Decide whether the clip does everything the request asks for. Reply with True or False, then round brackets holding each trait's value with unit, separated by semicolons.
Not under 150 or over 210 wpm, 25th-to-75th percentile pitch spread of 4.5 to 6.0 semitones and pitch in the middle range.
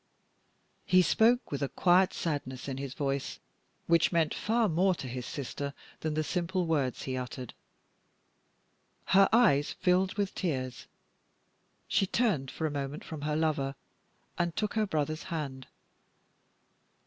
False (140 wpm; 5.0 semitones; 155 Hz)